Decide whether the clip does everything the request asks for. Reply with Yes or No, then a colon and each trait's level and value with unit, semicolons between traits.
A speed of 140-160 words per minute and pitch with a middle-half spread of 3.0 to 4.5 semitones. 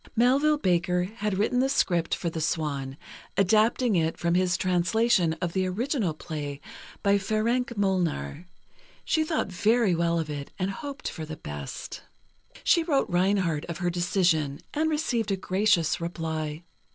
No: average, 150 wpm; average, 5.2 semitones